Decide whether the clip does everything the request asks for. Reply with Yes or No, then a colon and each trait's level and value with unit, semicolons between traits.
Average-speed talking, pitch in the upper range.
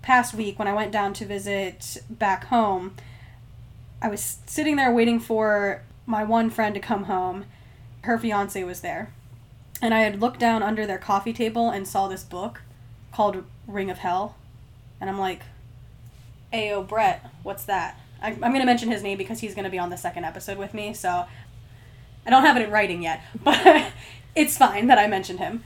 Yes: average, 195 wpm; high, 195 Hz